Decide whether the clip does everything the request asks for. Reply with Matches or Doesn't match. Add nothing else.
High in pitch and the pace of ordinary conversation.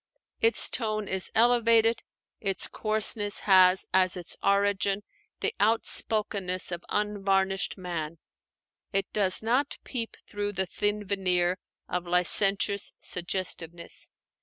Doesn't match